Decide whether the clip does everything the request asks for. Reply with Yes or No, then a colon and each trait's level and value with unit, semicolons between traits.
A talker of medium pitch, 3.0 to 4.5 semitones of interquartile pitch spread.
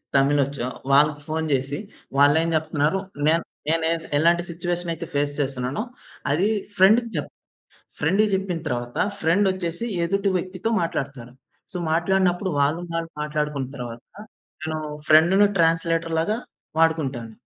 Yes: medium, 160 Hz; average, 3.6 semitones